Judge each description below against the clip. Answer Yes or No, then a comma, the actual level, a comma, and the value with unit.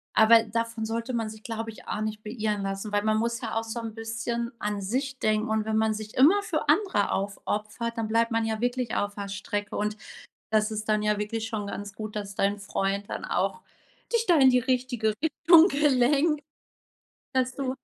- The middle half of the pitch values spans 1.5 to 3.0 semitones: Yes, narrow, 2.6 semitones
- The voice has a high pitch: Yes, high, 225 Hz